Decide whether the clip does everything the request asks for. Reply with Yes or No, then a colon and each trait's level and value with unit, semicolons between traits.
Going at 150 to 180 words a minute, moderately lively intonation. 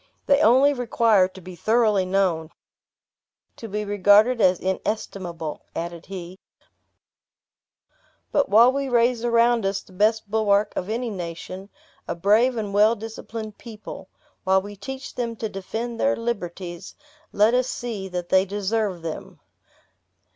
No: average, 140 wpm; average, 3.6 semitones